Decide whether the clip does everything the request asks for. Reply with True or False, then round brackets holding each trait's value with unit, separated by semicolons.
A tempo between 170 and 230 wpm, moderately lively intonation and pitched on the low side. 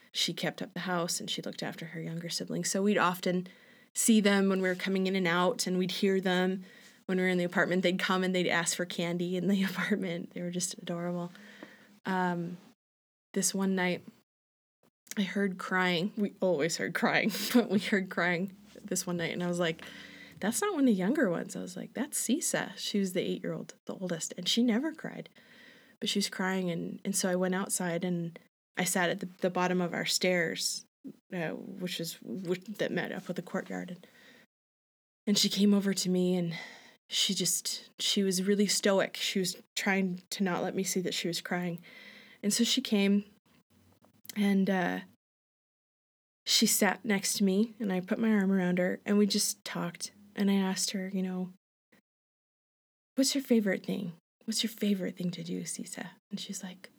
False (200 wpm; 3.2 semitones; 195 Hz)